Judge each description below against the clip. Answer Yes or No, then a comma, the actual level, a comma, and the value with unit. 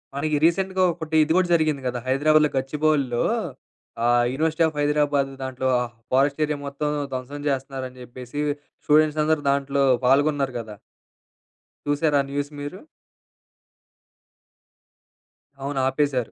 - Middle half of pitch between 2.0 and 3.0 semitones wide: Yes, narrow, 2.5 semitones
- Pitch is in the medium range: Yes, medium, 145 Hz